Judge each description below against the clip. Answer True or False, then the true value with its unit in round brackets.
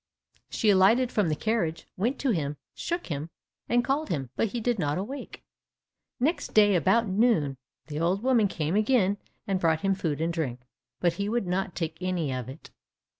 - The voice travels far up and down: True (6.0 semitones)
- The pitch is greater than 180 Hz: True (190 Hz)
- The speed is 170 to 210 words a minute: True (185 wpm)